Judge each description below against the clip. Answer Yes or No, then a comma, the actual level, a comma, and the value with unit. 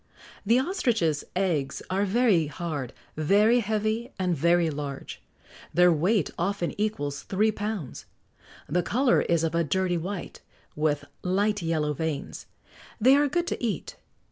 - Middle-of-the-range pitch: Yes, medium, 180 Hz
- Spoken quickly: No, average, 140 wpm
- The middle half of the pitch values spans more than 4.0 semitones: Yes, wide, 5.4 semitones